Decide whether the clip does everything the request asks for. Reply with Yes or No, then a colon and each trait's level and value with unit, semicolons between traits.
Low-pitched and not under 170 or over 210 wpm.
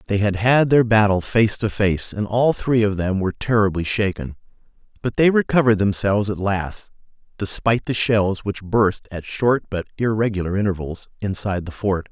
Yes: low, 105 Hz; average, 175 wpm